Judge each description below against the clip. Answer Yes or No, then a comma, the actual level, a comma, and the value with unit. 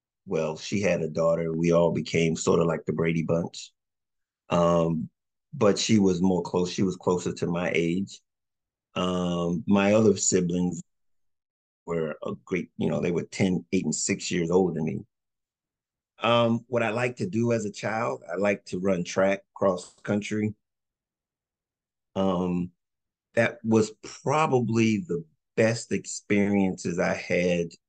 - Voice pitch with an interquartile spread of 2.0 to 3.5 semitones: No, average, 3.9 semitones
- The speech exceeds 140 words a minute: Yes, average, 150 wpm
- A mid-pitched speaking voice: No, very low, 95 Hz